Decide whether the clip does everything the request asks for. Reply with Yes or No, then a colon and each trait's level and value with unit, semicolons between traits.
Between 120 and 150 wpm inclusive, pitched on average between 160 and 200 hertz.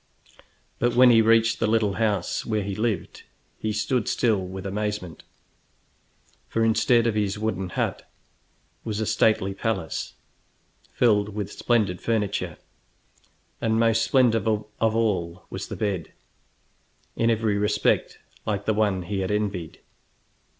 No: slow, 135 wpm; low, 105 Hz